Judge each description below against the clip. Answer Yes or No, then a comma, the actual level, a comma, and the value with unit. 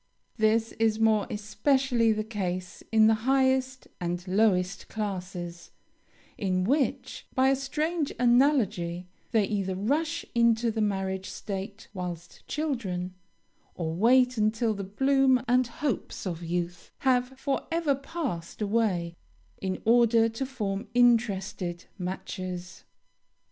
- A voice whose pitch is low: No, high, 220 Hz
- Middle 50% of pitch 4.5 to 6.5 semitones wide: Yes, average, 5.3 semitones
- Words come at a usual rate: No, slow, 115 wpm